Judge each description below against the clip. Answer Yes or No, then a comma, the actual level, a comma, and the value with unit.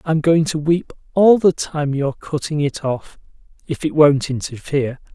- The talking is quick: No, average, 175 wpm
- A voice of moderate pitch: Yes, medium, 150 Hz